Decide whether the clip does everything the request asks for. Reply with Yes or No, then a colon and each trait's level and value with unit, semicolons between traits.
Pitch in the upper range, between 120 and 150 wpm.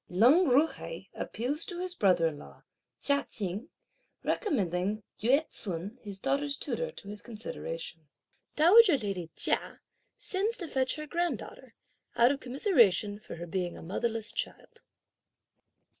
Yes: high, 240 Hz; average, 140 wpm